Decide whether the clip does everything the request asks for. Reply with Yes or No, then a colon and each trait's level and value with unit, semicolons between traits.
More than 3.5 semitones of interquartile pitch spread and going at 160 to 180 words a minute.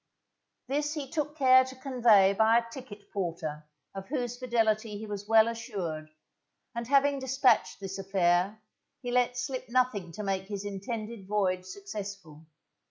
No: average, 4.5 semitones; average, 150 wpm